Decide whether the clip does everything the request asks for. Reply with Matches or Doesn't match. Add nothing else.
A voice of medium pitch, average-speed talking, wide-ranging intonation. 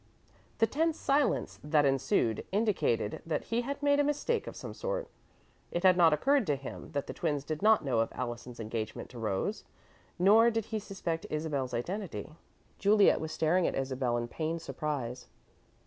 Matches